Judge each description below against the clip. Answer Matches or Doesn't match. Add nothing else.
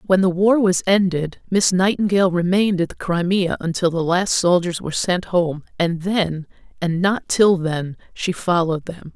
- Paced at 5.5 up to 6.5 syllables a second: Doesn't match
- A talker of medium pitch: Matches